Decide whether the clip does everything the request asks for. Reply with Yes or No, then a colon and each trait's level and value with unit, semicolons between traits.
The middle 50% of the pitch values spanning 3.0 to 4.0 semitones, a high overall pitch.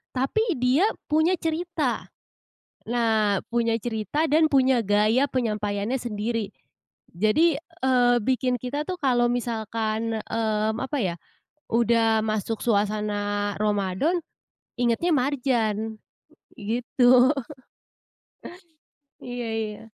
Yes: average, 3.5 semitones; high, 235 Hz